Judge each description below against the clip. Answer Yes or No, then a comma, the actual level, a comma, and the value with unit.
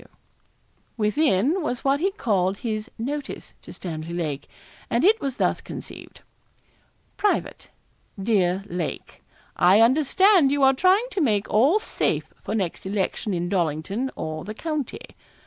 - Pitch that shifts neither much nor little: No, wide, 7.7 semitones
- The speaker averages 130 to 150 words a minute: Yes, average, 140 wpm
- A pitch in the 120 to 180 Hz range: No, high, 225 Hz